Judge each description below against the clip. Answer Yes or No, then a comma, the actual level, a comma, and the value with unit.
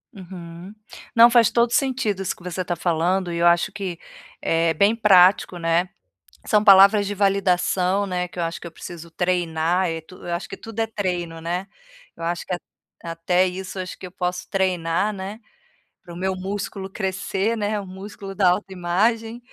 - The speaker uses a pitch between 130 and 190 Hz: Yes, medium, 185 Hz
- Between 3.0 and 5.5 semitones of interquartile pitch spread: No, narrow, 2.6 semitones